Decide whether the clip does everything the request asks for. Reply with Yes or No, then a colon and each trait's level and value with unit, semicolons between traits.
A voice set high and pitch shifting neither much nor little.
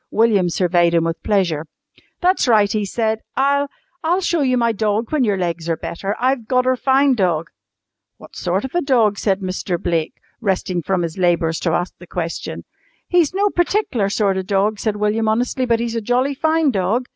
No: high, 215 Hz; wide, 5.8 semitones